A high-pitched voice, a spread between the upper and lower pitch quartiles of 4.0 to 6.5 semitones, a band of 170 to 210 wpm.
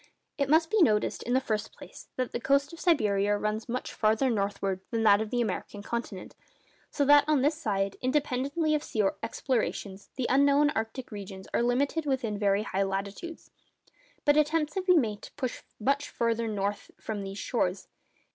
Yes: high, 235 Hz; wide, 5.5 semitones; average, 180 wpm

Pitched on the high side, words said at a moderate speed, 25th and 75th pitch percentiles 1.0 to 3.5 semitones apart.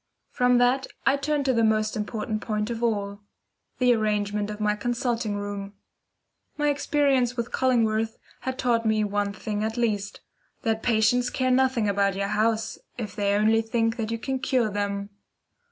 Yes: high, 225 Hz; average, 170 wpm; average, 2.9 semitones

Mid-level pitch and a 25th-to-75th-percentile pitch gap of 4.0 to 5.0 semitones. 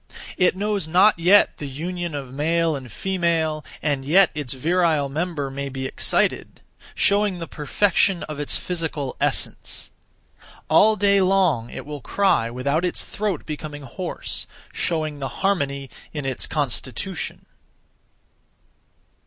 Yes: medium, 155 Hz; average, 4.7 semitones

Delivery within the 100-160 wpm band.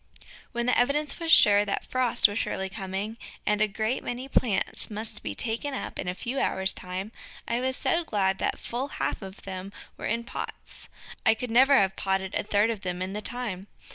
No: fast, 205 wpm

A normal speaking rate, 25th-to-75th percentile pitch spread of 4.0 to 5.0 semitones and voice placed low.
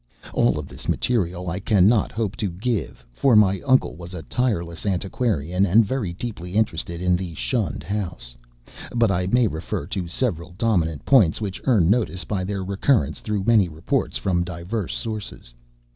Yes: average, 165 wpm; average, 4.3 semitones; very low, 95 Hz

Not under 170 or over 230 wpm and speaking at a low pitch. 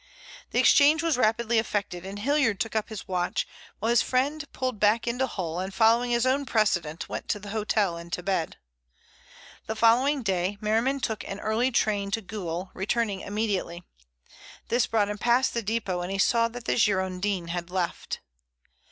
No: average, 180 wpm; high, 215 Hz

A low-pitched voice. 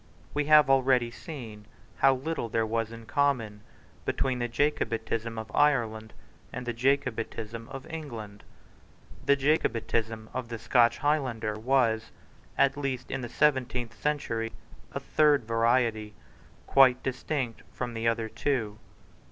Yes: low, 120 Hz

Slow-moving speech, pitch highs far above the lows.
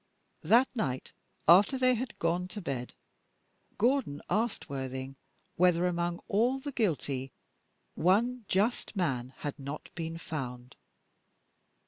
Yes: slow, 115 wpm; wide, 8.2 semitones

